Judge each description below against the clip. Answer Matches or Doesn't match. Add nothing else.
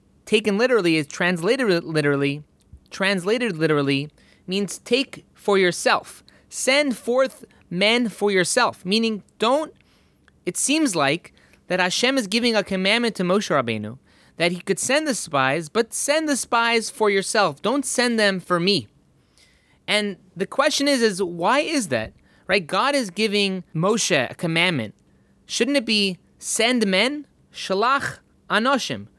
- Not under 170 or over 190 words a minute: Doesn't match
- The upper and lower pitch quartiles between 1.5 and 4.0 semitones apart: Doesn't match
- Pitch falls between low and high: Doesn't match